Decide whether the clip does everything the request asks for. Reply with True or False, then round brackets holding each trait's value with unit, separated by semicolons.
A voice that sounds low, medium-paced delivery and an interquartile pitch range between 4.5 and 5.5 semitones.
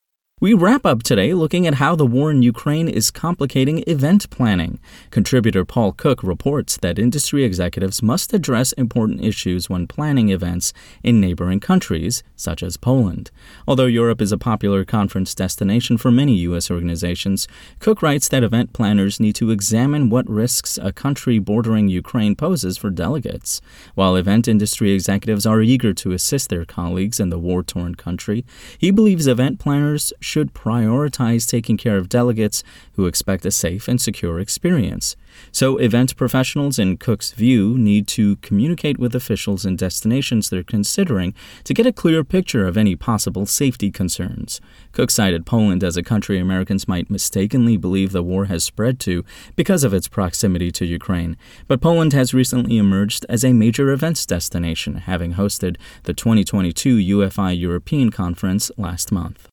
True (105 Hz; 160 wpm; 5.2 semitones)